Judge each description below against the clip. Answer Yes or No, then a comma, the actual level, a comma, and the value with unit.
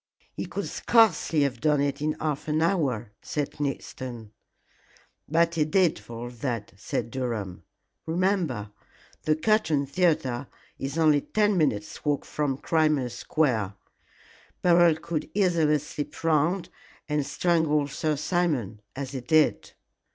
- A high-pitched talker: No, medium, 150 Hz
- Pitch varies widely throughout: No, average, 4.0 semitones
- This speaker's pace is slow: Yes, slow, 130 wpm